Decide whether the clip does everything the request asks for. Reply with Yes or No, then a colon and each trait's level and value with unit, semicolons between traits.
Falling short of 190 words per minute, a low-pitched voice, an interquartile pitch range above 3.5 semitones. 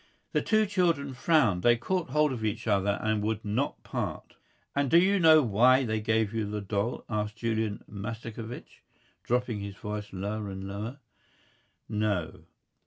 Yes: average, 160 wpm; low, 110 Hz; average, 4.1 semitones